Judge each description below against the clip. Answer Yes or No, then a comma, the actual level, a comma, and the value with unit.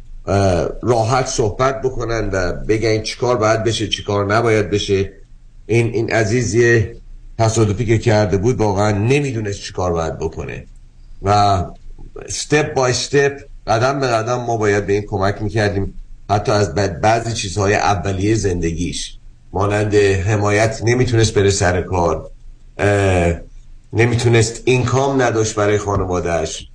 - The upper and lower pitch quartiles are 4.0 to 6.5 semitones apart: No, average, 2.8 semitones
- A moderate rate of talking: Yes, average, 120 wpm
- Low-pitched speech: Yes, low, 105 Hz